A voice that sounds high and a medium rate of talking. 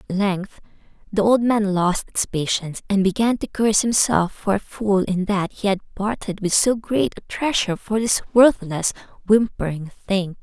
Yes: high, 200 Hz; average, 175 wpm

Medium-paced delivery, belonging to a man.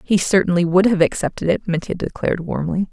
No: average, 185 wpm; female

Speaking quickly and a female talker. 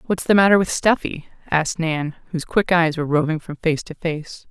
Yes: fast, 215 wpm; female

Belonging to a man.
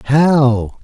Yes: male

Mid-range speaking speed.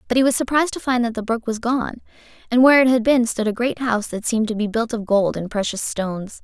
No: fast, 280 wpm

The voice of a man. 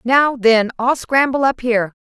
No: female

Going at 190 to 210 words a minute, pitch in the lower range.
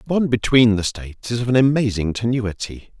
Yes: average, 200 wpm; low, 115 Hz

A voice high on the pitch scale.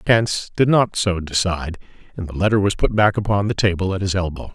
No: very low, 95 Hz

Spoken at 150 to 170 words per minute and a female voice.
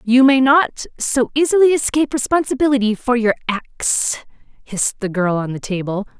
Yes: average, 155 wpm; female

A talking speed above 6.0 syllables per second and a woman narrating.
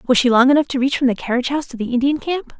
Yes: 7.5 syllables/s; female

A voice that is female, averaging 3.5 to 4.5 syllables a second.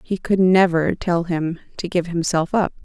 Yes: female; 4.4 syllables/s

